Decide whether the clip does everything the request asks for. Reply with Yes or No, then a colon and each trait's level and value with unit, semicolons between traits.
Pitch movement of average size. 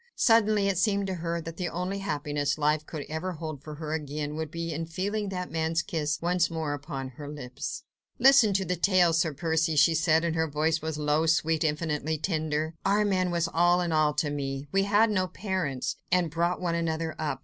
Yes: average, 3.0 semitones